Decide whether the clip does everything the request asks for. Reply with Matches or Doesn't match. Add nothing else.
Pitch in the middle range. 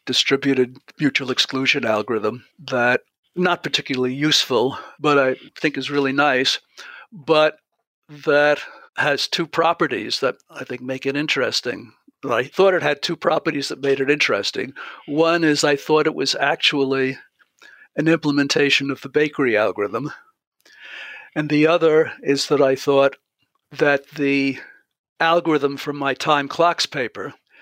Matches